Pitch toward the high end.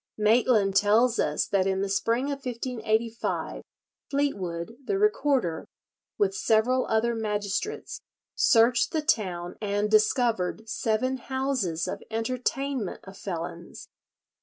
Yes: high, 225 Hz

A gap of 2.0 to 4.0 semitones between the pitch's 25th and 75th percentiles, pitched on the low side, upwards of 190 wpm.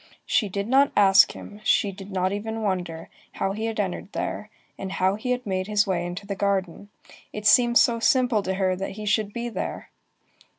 No: narrow, 2.6 semitones; high, 200 Hz; fast, 205 wpm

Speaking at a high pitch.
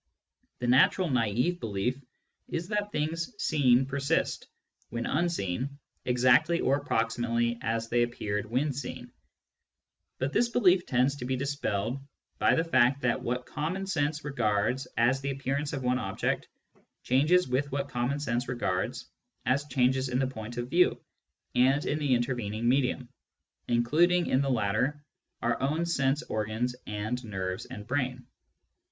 No: low, 130 Hz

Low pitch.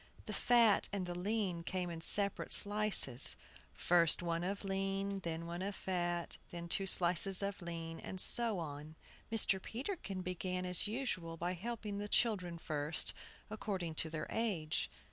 No: medium, 185 Hz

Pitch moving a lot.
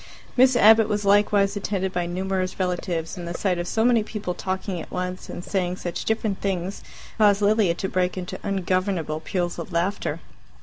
No: narrow, 2.4 semitones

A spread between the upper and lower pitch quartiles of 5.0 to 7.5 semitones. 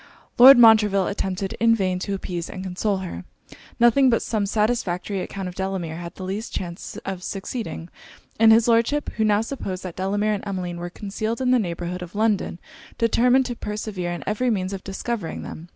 No: average, 3.6 semitones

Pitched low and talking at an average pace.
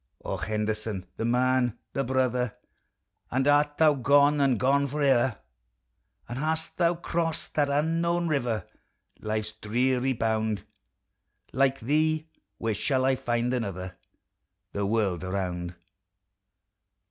No: low, 130 Hz; slow, 115 wpm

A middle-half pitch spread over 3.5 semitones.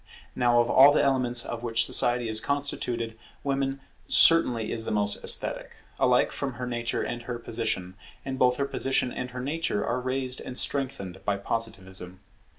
No: average, 2.7 semitones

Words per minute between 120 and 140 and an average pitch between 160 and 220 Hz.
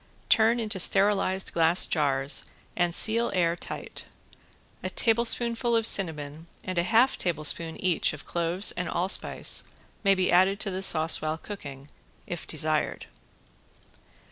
Yes: slow, 135 wpm; medium, 185 Hz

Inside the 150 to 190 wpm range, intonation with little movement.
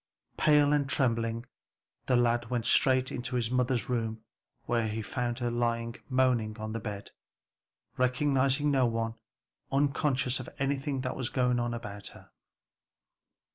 No: average, 140 wpm; narrow, 2.3 semitones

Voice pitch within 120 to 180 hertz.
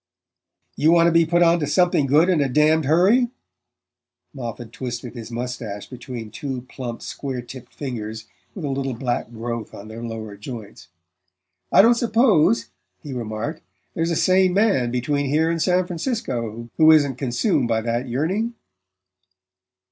Yes: low, 135 Hz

